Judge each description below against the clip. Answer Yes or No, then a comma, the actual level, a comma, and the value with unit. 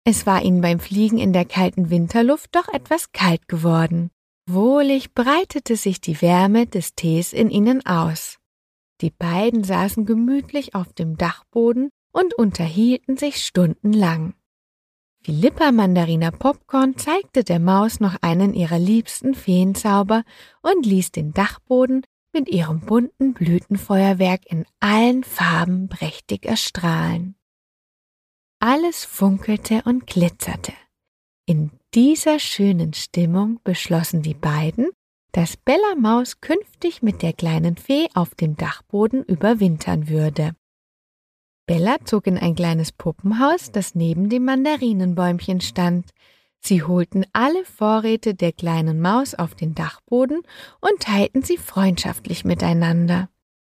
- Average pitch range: No, wide, 6.1 semitones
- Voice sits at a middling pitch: No, high, 195 Hz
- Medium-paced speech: No, slow, 120 wpm